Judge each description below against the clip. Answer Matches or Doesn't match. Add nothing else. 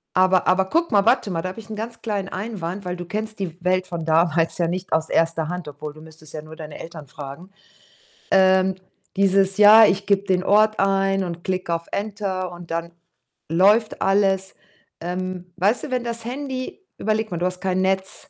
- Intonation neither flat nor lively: Matches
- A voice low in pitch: Doesn't match